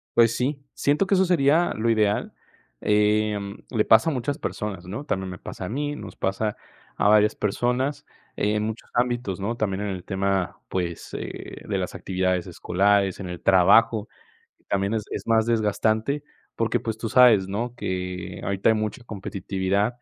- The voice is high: No, low, 105 Hz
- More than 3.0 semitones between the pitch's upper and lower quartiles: Yes, average, 3.4 semitones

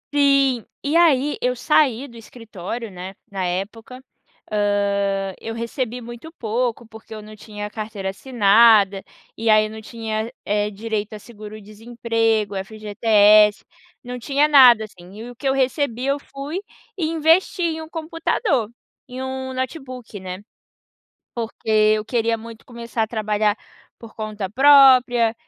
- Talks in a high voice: Yes, high, 230 Hz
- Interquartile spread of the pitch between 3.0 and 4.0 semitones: Yes, average, 3.6 semitones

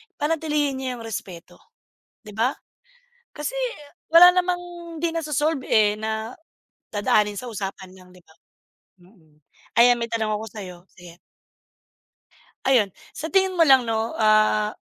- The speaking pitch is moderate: No, high, 230 Hz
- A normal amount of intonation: No, wide, 6.4 semitones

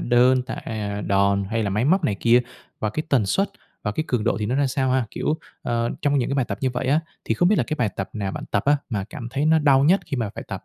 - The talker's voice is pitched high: No, low, 125 Hz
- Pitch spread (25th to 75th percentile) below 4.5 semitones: No, average, 5.0 semitones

